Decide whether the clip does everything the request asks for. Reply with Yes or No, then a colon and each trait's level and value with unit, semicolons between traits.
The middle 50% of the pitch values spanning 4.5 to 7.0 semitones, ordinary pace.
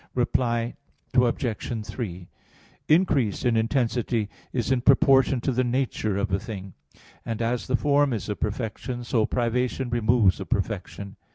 No: average, 2.9 semitones; average, 145 wpm